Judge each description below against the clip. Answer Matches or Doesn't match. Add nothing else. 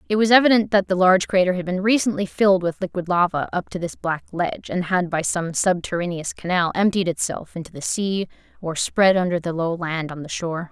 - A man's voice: Doesn't match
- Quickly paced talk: Matches